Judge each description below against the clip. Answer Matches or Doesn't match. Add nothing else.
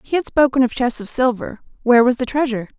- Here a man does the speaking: Doesn't match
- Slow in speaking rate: Doesn't match